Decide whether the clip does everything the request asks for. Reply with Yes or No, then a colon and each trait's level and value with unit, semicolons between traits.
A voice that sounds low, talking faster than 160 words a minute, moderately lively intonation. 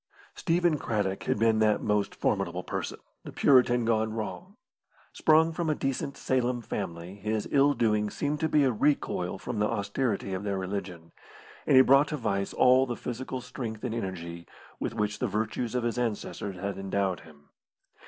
Yes: low, 110 Hz; average, 175 wpm; average, 4.6 semitones